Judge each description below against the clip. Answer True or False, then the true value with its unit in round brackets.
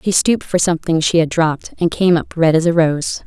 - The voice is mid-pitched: True (165 Hz)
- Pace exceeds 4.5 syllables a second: True (5.8 syllables/s)